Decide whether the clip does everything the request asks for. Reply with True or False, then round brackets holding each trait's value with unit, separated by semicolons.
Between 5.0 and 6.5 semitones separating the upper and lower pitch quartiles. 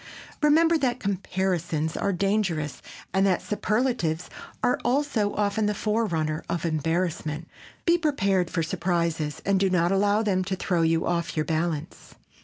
False (4.2 semitones)